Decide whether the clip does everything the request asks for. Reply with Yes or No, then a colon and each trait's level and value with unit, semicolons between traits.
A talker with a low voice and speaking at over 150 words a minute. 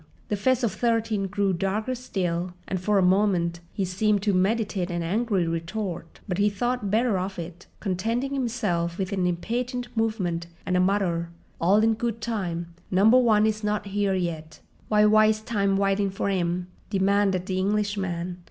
No: high, 200 Hz; average, 170 wpm